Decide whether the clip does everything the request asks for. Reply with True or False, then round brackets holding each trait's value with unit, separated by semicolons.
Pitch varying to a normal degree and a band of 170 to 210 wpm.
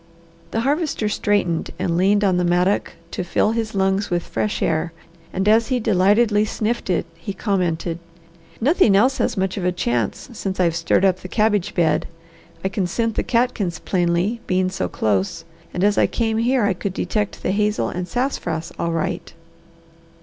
True (3.6 semitones; 180 wpm)